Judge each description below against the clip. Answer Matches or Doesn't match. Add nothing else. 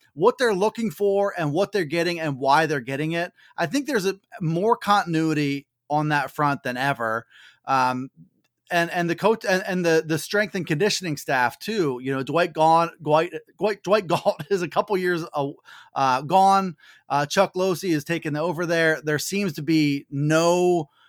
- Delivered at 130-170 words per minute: Doesn't match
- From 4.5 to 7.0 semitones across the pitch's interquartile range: Matches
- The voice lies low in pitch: Doesn't match